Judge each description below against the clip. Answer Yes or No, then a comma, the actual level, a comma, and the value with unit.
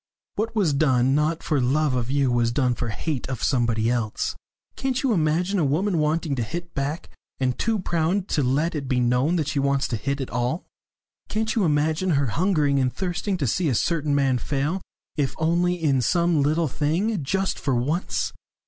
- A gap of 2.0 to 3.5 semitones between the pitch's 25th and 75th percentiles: No, average, 4.7 semitones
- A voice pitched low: No, medium, 150 Hz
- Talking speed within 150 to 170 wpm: No, average, 195 wpm